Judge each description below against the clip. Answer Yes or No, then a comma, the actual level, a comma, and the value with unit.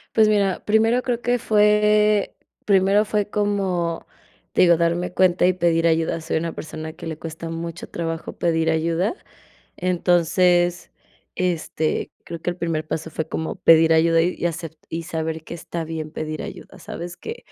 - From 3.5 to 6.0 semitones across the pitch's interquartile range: No, average, 2.9 semitones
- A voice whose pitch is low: No, medium, 170 Hz